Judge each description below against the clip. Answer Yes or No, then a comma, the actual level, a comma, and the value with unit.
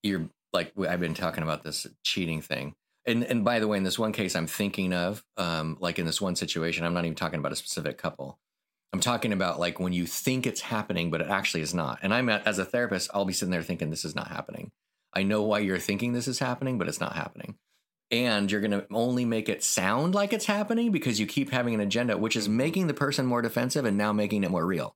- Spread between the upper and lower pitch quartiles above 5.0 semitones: Yes, wide, 5.6 semitones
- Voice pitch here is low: Yes, low, 105 Hz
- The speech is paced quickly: Yes, fast, 255 wpm